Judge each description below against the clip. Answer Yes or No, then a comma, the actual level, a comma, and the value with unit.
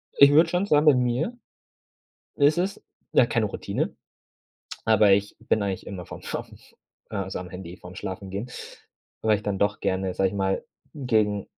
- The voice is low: Yes, low, 105 Hz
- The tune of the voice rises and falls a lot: Yes, wide, 6.7 semitones